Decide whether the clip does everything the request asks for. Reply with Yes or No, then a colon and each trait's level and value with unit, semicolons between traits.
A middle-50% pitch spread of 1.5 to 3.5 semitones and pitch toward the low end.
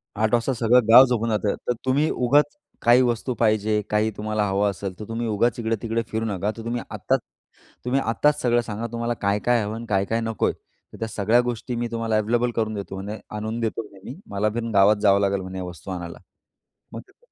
Yes: narrow, 2.4 semitones; low, 110 Hz